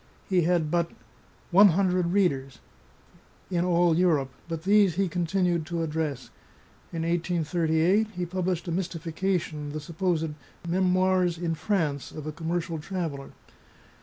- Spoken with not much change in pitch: Yes, narrow, 2.3 semitones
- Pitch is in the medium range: Yes, medium, 170 Hz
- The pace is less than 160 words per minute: Yes, average, 140 wpm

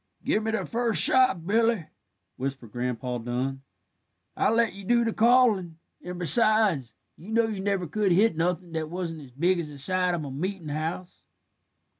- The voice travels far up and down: Yes, wide, 6.2 semitones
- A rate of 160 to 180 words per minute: Yes, average, 170 wpm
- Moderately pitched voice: Yes, medium, 180 Hz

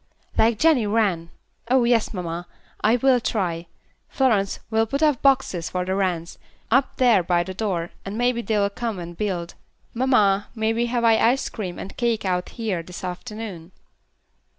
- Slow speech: No, average, 175 wpm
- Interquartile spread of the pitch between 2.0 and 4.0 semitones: No, average, 4.7 semitones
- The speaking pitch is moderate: No, high, 210 Hz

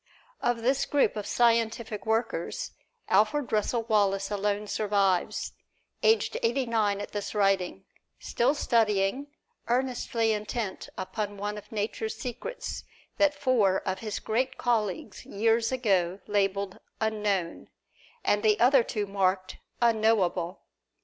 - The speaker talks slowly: Yes, slow, 120 wpm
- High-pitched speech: Yes, high, 215 Hz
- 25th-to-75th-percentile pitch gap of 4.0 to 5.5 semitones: No, average, 2.9 semitones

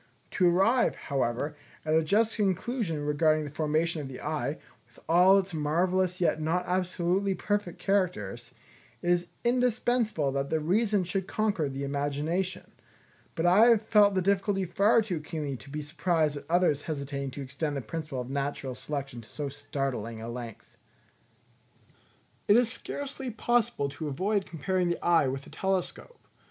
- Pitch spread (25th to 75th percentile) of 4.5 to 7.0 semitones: Yes, average, 5.2 semitones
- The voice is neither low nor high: Yes, medium, 165 Hz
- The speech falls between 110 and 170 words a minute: Yes, average, 160 wpm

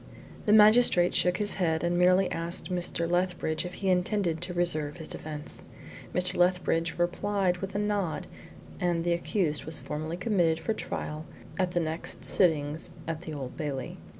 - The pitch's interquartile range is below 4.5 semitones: Yes, narrow, 2.4 semitones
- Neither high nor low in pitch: Yes, medium, 175 Hz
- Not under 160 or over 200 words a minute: Yes, average, 165 wpm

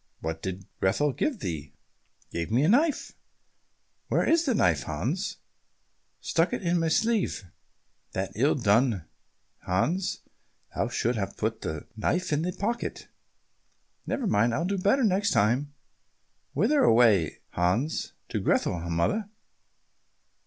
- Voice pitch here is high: No, medium, 145 Hz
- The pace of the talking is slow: Yes, slow, 130 wpm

